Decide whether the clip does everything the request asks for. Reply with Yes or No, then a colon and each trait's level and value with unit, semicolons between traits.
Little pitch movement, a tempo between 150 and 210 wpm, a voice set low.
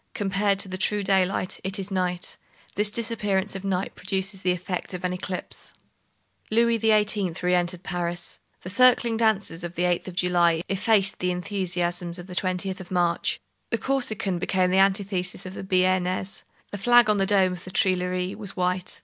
No: narrow, 2.0 semitones; average, 180 wpm; medium, 185 Hz